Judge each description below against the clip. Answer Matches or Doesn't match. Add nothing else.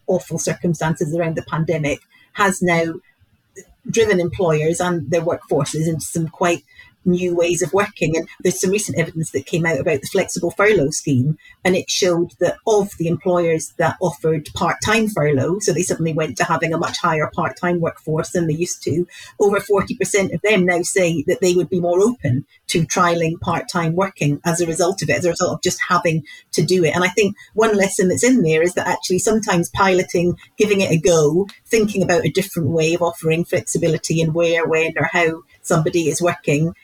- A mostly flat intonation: Matches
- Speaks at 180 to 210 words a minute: Matches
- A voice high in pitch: Doesn't match